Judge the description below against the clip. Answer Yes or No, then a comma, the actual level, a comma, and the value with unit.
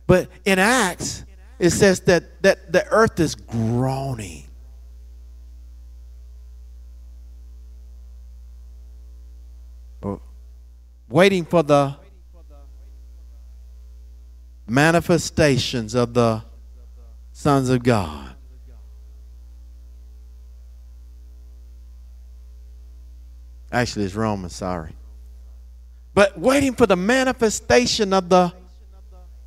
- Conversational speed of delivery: No, slow, 65 wpm